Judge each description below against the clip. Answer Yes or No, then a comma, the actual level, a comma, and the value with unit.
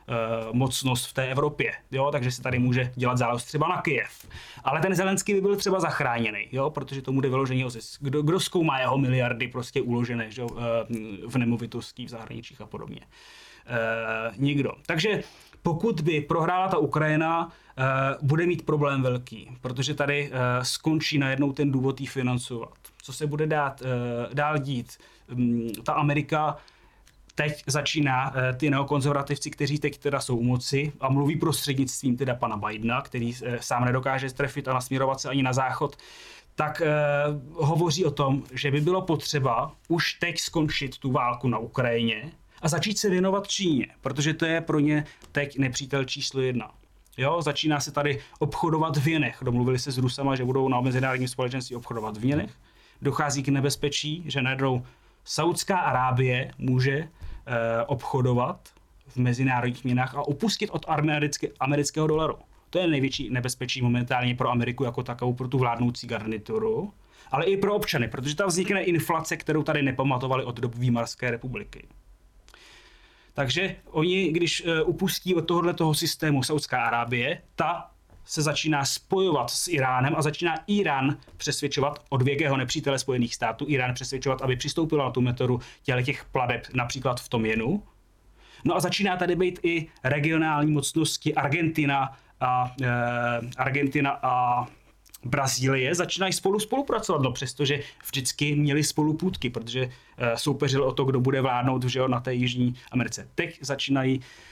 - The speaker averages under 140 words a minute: No, average, 155 wpm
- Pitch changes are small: No, average, 3.6 semitones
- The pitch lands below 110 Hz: No, low, 135 Hz